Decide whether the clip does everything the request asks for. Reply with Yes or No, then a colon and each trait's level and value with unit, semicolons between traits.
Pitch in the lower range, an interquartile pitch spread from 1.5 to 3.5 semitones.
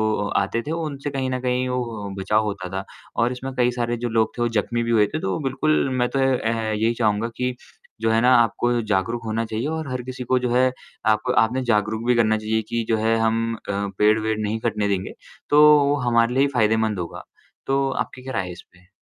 Yes: low, 115 Hz; average, 2.7 semitones